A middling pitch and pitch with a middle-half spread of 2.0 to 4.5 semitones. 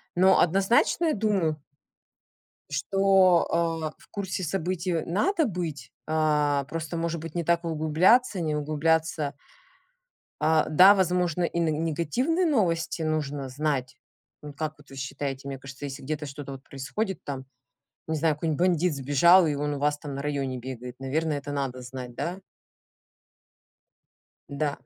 Yes: medium, 155 Hz; average, 3.6 semitones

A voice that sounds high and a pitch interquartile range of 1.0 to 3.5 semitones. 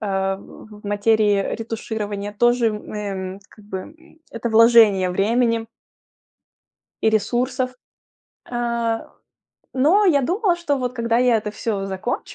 Yes: high, 225 Hz; average, 3.1 semitones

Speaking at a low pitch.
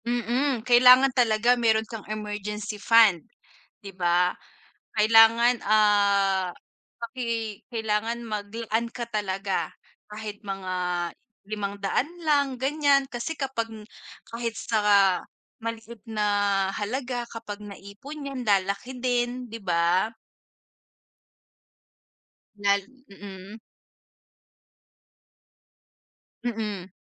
No: high, 220 Hz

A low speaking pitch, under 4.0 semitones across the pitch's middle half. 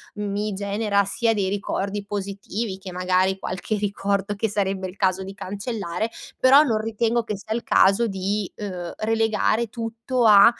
No: high, 205 Hz; narrow, 2.5 semitones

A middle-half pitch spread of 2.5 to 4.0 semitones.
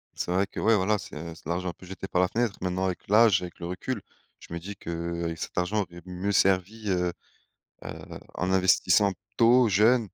Yes: average, 2.8 semitones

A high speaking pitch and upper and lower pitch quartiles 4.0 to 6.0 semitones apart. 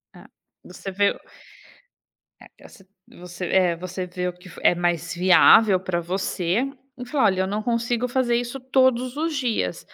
Yes: high, 195 Hz; average, 5.2 semitones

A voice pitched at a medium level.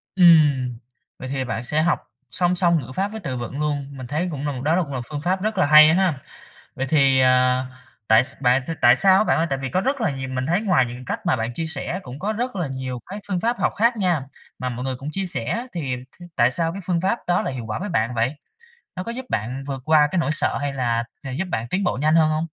Yes: medium, 150 Hz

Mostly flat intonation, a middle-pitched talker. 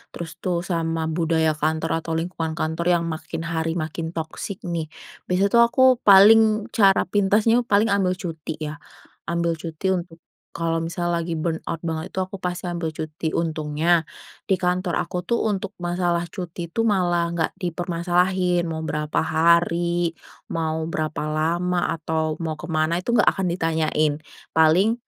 Yes: narrow, 2.0 semitones; medium, 170 Hz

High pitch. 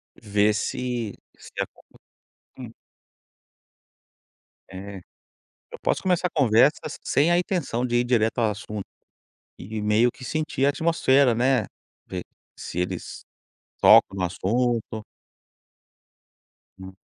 No: low, 120 Hz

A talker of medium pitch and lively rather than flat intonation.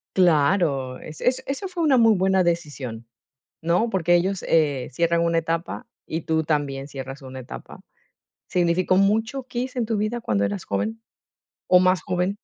Yes: medium, 170 Hz; wide, 5.7 semitones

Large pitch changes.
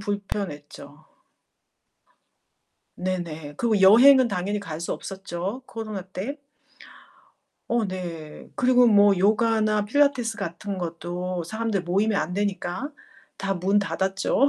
No: average, 3.6 semitones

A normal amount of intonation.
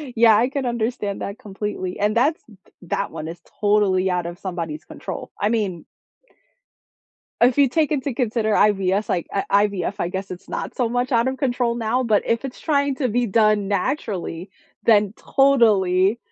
Yes: average, 4.4 semitones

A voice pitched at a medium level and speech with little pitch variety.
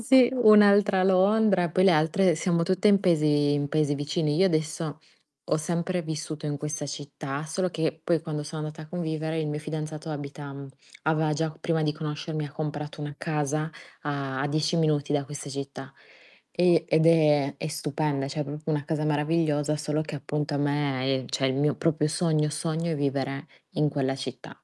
Yes: medium, 155 Hz; narrow, 1.9 semitones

